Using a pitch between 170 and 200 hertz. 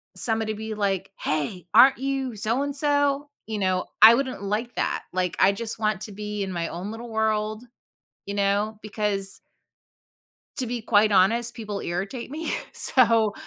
No: high, 215 Hz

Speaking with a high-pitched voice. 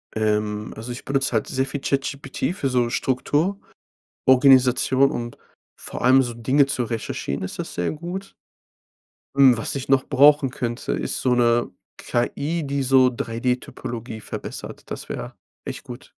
No: low, 130 Hz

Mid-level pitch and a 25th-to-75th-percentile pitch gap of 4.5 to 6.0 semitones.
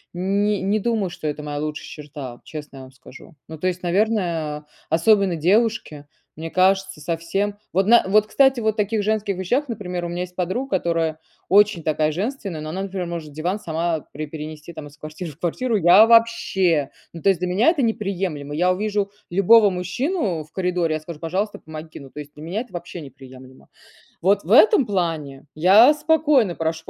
Yes: medium, 180 Hz; average, 4.9 semitones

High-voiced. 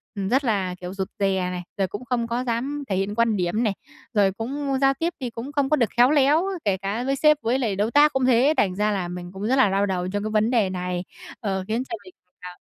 Yes: high, 215 Hz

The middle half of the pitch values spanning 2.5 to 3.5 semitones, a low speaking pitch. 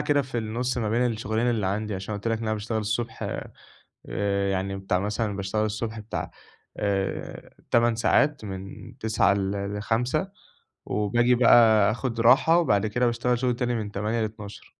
Yes: average, 2.8 semitones; low, 110 Hz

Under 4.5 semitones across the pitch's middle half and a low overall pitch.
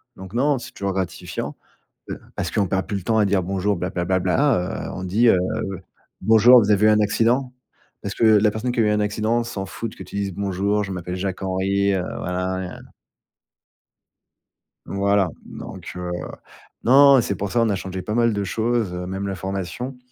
Yes: average, 3.1 semitones; low, 100 Hz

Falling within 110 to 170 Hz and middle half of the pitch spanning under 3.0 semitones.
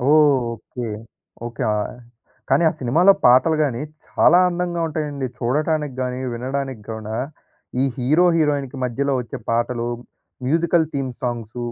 No: low, 135 Hz; average, 4.2 semitones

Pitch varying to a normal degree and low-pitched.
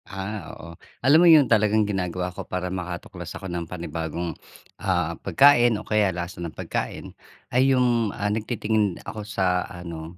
Yes: average, 4.1 semitones; very low, 95 Hz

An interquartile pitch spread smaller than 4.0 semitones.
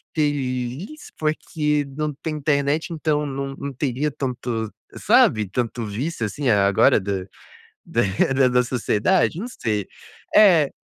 No: average, 4.4 semitones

